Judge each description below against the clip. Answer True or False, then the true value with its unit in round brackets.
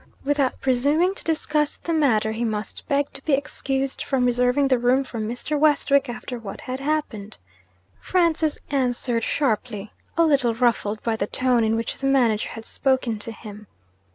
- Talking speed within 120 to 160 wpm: False (170 wpm)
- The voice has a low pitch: False (255 Hz)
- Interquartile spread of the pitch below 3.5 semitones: False (3.9 semitones)